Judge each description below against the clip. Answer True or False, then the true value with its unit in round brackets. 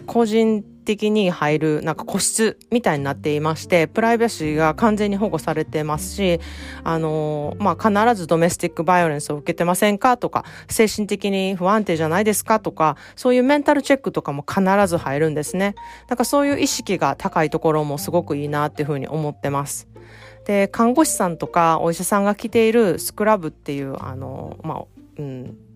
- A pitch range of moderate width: False (6.1 semitones)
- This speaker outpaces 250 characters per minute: True (405 characters per minute)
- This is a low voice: False (170 Hz)